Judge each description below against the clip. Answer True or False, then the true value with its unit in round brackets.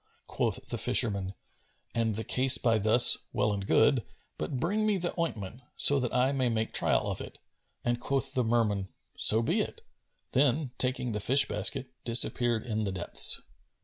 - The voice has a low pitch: True (120 Hz)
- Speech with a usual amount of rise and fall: True (3.7 semitones)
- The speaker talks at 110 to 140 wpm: False (175 wpm)